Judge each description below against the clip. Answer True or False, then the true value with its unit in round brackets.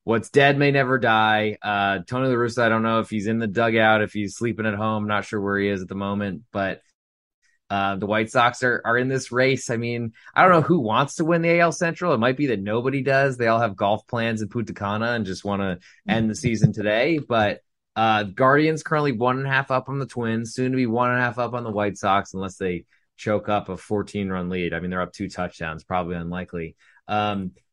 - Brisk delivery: True (245 wpm)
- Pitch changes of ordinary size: True (4.0 semitones)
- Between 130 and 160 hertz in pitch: False (110 Hz)